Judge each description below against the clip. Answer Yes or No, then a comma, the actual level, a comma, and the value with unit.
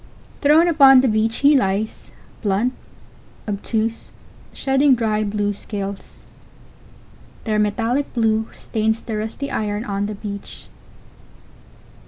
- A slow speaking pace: Yes, slow, 110 wpm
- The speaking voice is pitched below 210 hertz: No, high, 220 Hz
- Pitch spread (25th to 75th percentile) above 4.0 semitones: No, average, 3.4 semitones